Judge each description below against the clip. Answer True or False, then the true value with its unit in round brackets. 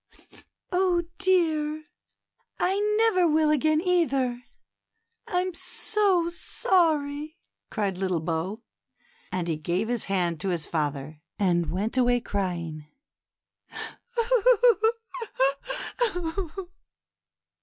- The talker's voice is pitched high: True (245 Hz)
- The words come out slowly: True (85 wpm)